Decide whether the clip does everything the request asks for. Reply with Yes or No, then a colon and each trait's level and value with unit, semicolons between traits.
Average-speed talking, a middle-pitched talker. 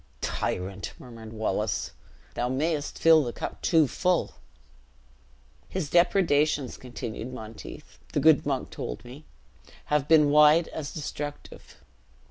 No: slow, 115 wpm; medium, 145 Hz